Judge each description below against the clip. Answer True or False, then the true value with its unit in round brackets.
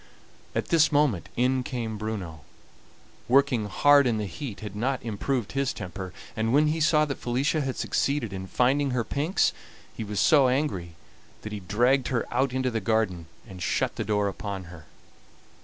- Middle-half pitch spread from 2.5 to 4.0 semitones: False (5.2 semitones)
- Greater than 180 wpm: False (175 wpm)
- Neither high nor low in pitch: False (120 Hz)